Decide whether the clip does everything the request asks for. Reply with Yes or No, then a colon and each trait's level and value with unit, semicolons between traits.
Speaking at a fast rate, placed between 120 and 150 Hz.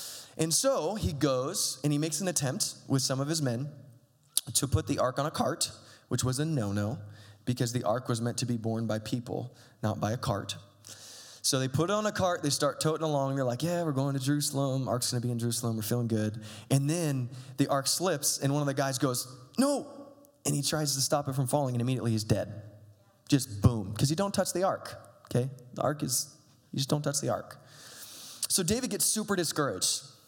Yes: fast, 225 wpm; low, 135 Hz